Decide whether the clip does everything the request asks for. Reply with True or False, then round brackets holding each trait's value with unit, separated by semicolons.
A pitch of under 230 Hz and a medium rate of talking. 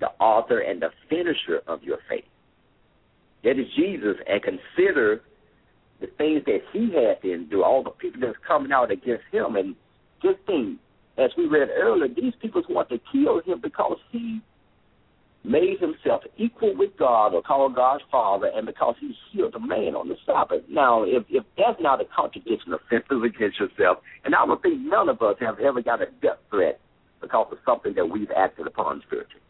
False (360 Hz; 185 wpm)